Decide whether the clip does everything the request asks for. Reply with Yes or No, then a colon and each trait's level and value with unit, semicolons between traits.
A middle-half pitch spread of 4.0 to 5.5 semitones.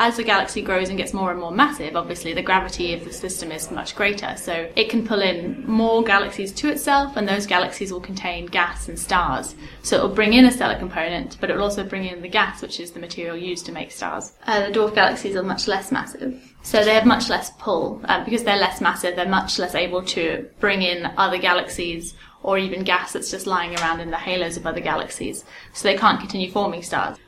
No: average, 3.1 semitones